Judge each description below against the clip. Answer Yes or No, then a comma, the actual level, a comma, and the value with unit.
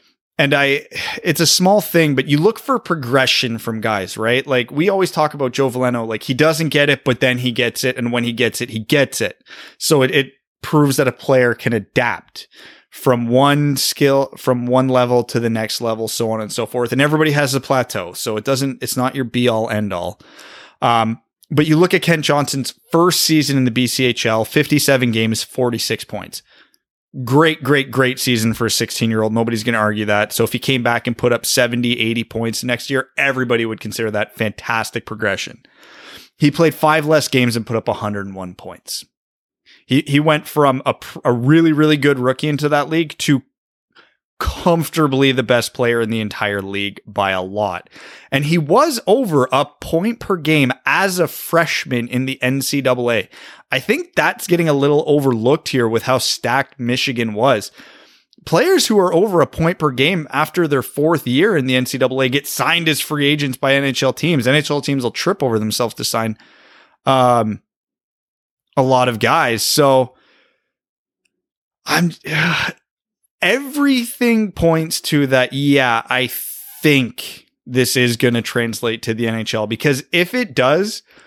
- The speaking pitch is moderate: No, low, 130 Hz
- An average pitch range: Yes, average, 4.2 semitones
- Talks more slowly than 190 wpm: Yes, average, 180 wpm